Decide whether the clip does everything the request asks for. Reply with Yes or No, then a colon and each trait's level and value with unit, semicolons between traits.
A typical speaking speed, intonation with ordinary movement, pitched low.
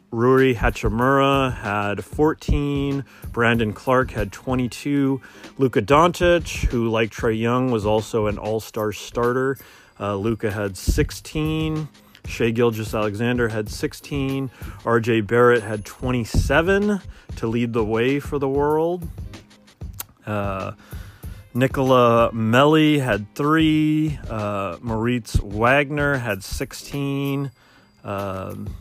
No: slow, 105 wpm; average, 4.6 semitones; low, 120 Hz